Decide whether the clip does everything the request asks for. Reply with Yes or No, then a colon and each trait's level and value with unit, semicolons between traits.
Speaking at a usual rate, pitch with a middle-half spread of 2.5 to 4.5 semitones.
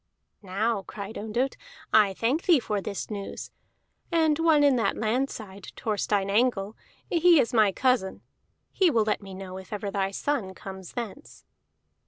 No: average, 160 wpm; average, 5.1 semitones